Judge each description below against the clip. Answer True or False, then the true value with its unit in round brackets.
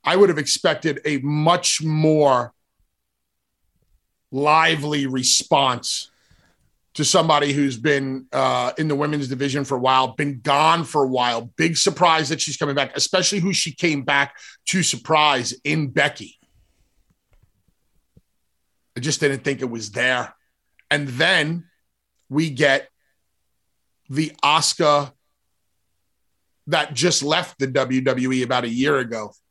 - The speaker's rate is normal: False (130 wpm)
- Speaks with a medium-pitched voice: True (145 Hz)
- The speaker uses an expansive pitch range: False (3.3 semitones)